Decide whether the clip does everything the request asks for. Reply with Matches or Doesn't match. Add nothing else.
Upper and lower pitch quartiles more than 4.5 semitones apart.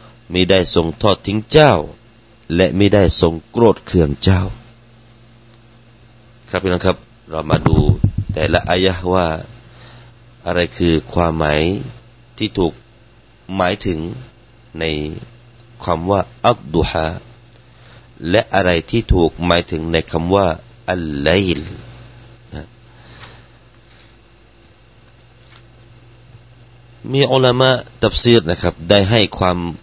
Matches